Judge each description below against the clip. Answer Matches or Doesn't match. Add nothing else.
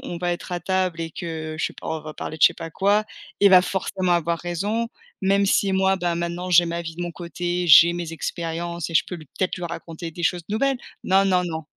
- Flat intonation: Matches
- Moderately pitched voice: Matches